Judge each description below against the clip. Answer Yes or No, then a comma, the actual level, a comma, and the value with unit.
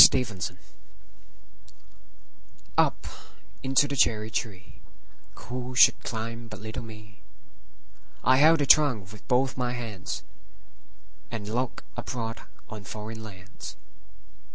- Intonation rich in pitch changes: No, average, 2.9 semitones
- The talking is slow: Yes, slow, 105 wpm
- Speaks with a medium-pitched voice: No, low, 115 Hz